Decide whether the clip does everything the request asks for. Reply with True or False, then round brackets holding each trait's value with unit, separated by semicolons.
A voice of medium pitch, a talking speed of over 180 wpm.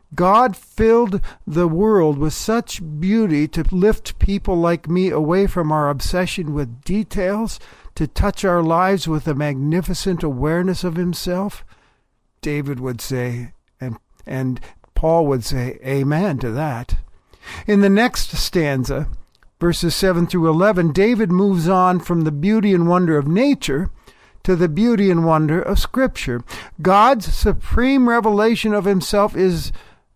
False (175 Hz; 140 wpm)